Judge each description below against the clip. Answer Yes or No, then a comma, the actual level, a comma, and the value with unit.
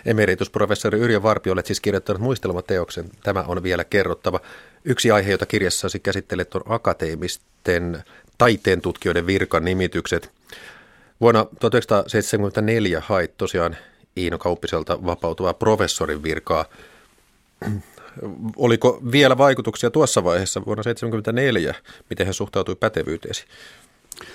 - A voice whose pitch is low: Yes, low, 100 Hz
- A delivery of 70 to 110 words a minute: Yes, average, 105 wpm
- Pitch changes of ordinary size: Yes, average, 3.6 semitones